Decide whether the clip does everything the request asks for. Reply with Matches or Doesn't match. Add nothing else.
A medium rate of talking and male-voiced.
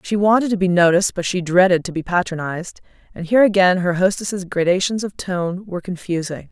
Doesn't match